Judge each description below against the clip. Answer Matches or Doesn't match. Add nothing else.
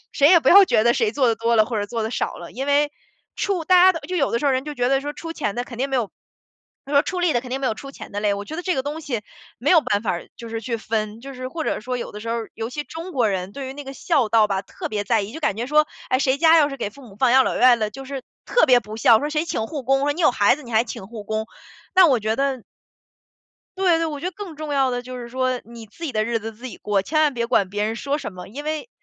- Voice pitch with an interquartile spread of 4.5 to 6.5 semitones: Matches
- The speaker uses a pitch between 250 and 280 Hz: Matches